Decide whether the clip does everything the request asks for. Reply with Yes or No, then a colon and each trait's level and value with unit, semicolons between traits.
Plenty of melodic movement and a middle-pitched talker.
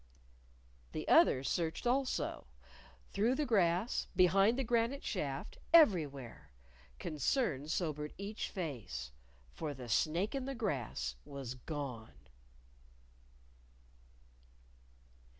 Yes: wide, 8.8 semitones; medium, 165 Hz